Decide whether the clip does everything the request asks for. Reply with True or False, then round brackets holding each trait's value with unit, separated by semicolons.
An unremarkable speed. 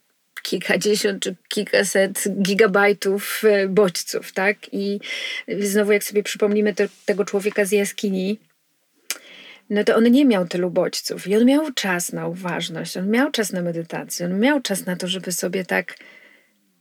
True (150 wpm)